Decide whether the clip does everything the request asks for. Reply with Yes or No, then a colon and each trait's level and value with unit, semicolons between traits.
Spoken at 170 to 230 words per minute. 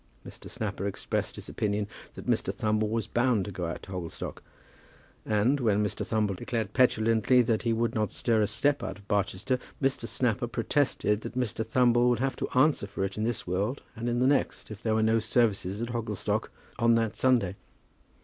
Yes: average, 195 wpm